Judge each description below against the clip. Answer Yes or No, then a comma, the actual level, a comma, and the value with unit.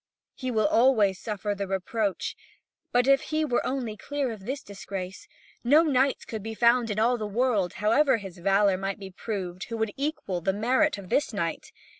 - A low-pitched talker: No, high, 220 Hz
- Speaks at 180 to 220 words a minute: Yes, average, 185 wpm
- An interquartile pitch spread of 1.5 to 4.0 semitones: No, average, 4.5 semitones